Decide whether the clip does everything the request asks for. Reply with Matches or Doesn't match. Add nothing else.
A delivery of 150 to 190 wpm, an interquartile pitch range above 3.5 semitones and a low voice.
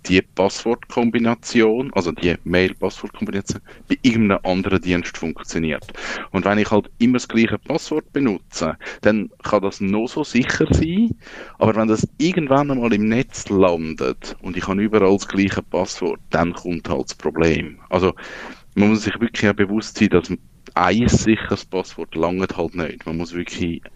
Matches